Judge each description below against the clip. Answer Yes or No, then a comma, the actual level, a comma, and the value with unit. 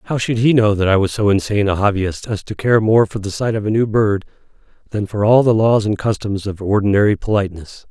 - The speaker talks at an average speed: No, fast, 245 wpm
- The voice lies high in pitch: No, low, 105 Hz